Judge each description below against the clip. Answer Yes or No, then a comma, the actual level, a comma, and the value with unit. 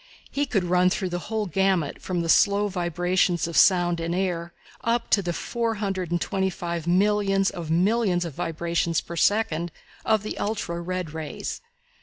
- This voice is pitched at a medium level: Yes, medium, 180 Hz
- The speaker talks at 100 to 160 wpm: No, average, 175 wpm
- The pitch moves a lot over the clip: No, average, 2.8 semitones